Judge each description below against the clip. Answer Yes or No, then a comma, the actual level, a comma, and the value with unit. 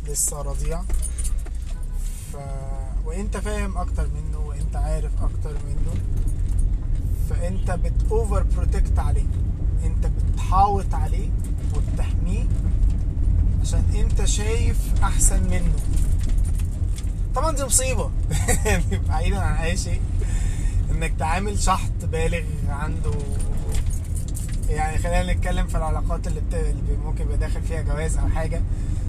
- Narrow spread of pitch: Yes, narrow, 1.7 semitones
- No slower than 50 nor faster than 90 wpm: No, average, 105 wpm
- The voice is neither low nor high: No, very low, 90 Hz